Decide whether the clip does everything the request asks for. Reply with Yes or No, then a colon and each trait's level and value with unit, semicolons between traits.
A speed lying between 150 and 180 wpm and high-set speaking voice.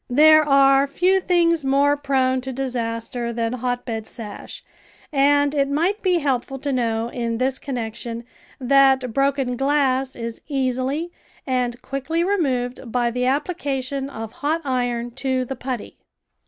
No: average, 140 wpm; very high, 265 Hz